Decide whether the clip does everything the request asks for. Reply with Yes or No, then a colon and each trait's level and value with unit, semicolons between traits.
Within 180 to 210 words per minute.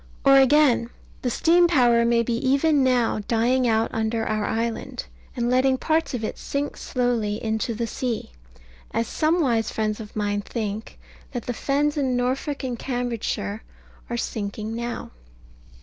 No: average, 155 wpm